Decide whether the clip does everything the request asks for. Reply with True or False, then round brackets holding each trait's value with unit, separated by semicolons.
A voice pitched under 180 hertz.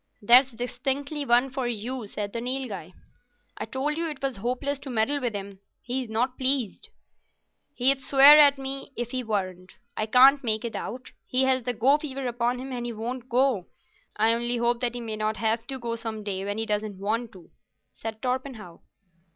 False (240 Hz)